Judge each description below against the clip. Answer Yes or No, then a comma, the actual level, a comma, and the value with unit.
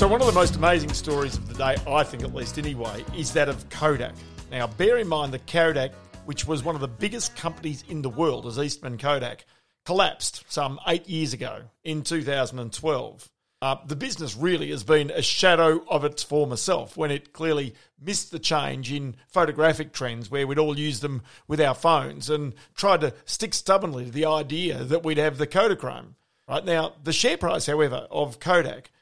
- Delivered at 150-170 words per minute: No, average, 195 wpm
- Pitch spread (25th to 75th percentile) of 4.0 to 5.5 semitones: No, average, 3.4 semitones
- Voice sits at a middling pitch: Yes, medium, 150 Hz